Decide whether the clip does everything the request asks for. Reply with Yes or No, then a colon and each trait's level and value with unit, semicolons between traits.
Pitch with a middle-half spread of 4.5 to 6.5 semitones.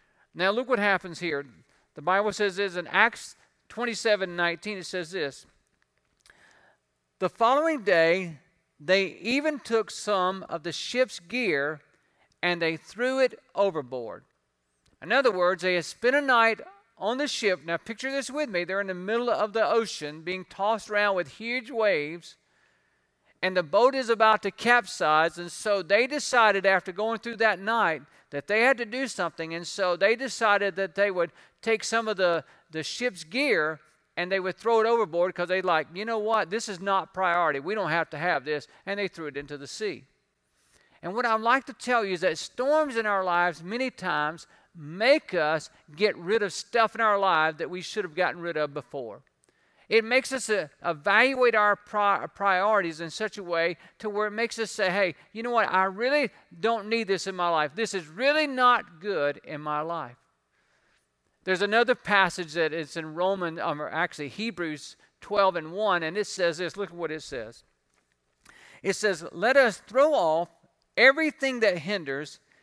Yes: average, 5.0 semitones